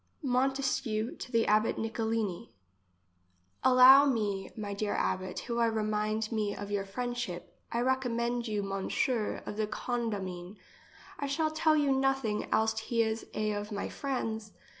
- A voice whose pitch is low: No, high, 220 Hz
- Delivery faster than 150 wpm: No, average, 145 wpm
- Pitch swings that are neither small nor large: Yes, average, 3.1 semitones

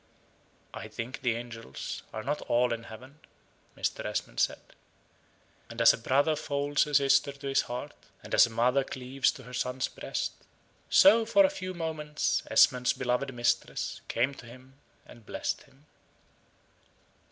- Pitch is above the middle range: No, low, 130 Hz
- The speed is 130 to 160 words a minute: Yes, average, 155 wpm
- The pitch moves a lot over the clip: No, average, 3.1 semitones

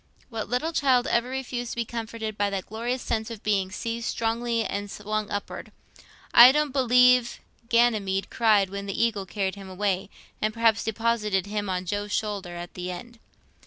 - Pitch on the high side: Yes, high, 220 Hz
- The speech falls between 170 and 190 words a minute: Yes, average, 175 wpm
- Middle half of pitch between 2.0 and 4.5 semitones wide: Yes, average, 2.9 semitones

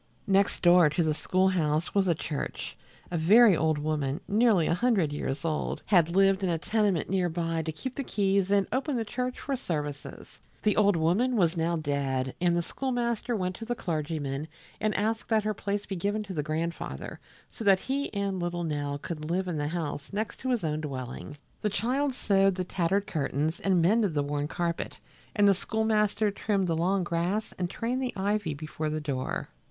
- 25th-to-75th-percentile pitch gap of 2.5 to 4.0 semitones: No, average, 4.8 semitones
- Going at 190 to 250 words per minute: Yes, average, 200 wpm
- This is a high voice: No, medium, 180 Hz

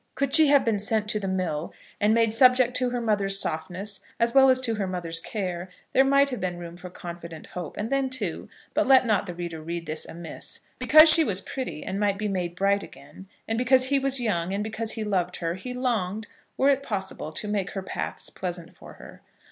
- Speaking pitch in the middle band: No, high, 205 Hz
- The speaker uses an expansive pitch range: Yes, wide, 5.9 semitones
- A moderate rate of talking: No, fast, 225 wpm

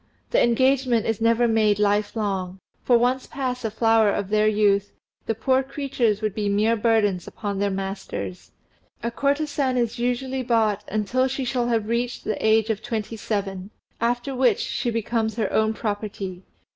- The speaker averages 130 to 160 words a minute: No, average, 170 wpm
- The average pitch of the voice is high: Yes, high, 225 Hz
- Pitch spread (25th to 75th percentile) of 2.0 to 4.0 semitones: Yes, average, 2.8 semitones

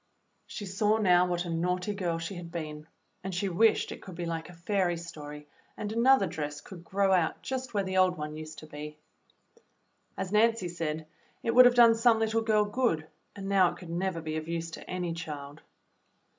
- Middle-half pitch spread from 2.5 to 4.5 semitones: Yes, average, 4.0 semitones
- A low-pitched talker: No, medium, 180 Hz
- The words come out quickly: Yes, fast, 220 wpm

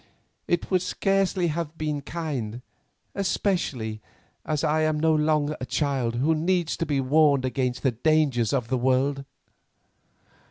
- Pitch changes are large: No, average, 3.7 semitones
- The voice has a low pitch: No, medium, 150 Hz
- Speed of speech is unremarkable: Yes, average, 145 wpm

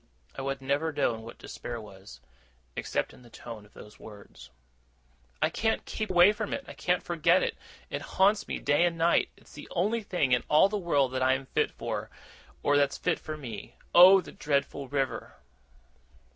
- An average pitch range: No, wide, 5.9 semitones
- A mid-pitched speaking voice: Yes, medium, 145 Hz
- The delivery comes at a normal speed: Yes, average, 190 wpm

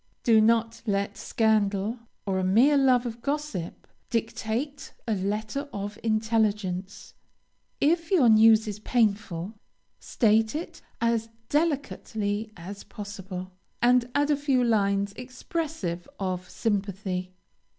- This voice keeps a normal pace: No, slow, 115 wpm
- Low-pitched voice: No, high, 220 Hz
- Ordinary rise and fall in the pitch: Yes, average, 3.8 semitones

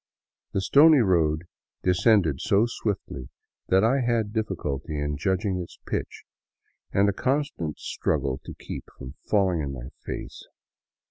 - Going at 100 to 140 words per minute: Yes, slow, 135 wpm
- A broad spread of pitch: Yes, wide, 6.4 semitones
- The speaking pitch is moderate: No, very low, 95 Hz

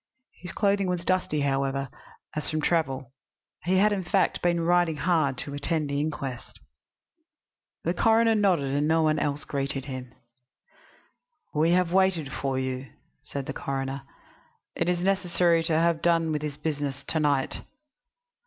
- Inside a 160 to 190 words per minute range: No, average, 150 wpm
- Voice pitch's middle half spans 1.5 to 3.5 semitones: No, average, 4.1 semitones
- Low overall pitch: No, medium, 155 Hz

